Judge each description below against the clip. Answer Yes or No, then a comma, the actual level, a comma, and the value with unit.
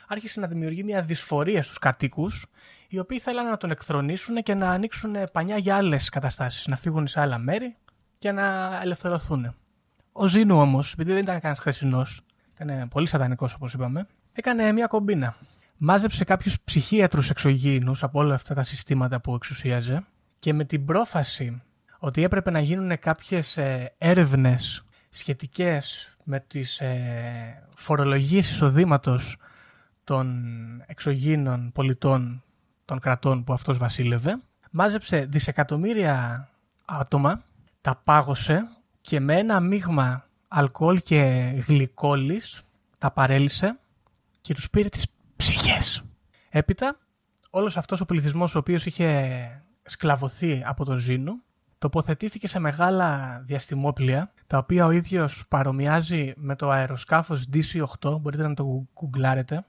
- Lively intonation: No, average, 5.0 semitones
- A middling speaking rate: Yes, average, 125 wpm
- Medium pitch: Yes, medium, 150 Hz